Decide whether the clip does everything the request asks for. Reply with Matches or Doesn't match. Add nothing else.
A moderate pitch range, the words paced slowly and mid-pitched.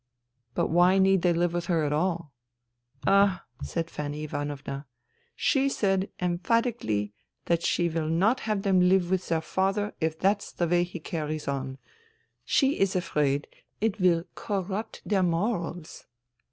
Doesn't match